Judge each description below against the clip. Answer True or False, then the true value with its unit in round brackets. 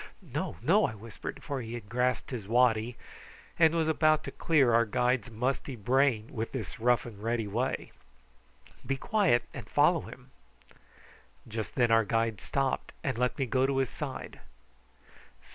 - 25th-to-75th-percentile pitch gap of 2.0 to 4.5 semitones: True (3.0 semitones)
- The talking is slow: False (160 wpm)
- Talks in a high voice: False (125 Hz)